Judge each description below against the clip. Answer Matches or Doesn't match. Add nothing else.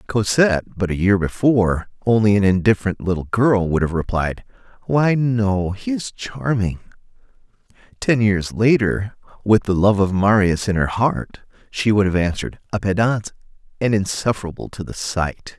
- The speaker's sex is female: Doesn't match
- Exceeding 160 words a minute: Doesn't match